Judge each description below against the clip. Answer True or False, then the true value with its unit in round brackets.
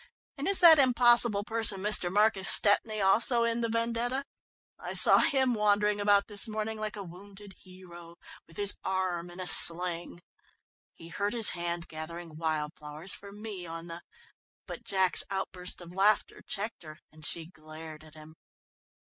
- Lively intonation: False (4.1 semitones)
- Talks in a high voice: True (195 Hz)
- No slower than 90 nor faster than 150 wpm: False (165 wpm)